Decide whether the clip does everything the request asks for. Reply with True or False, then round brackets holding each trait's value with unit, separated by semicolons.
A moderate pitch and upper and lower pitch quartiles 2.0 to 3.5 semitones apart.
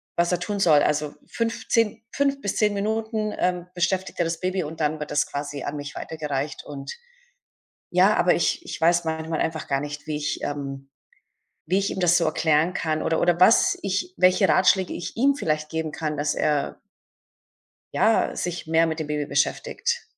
False (165 Hz; 4.2 semitones)